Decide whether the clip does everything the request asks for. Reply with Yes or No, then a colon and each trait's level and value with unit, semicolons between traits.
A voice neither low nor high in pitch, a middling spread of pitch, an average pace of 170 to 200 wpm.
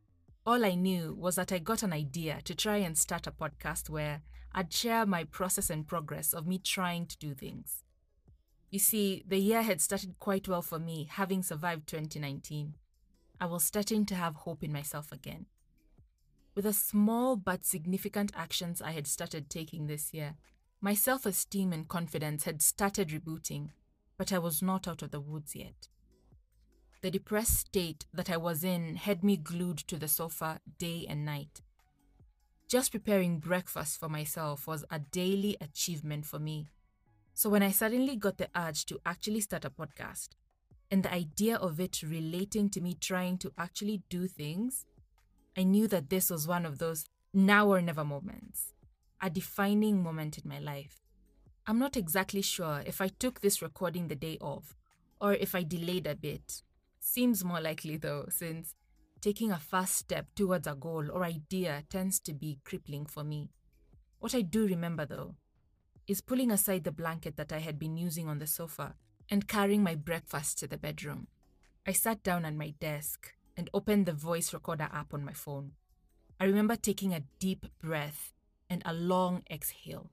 Yes: medium, 170 Hz; average, 4.1 semitones; average, 175 wpm